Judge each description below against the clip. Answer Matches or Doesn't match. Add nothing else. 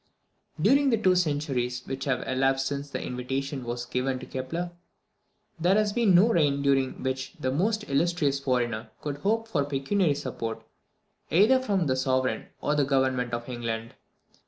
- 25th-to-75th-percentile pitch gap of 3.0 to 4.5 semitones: Doesn't match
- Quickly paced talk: Doesn't match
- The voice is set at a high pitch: Doesn't match